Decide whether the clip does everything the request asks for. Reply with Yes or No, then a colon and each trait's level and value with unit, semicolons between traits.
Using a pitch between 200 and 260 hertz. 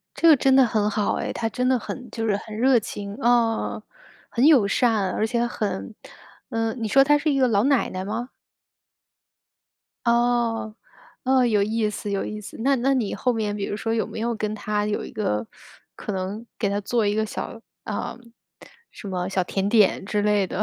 Yes: high, 220 Hz